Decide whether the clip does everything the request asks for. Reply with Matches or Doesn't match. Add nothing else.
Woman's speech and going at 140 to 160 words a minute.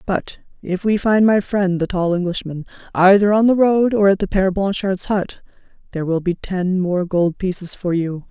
Doesn't match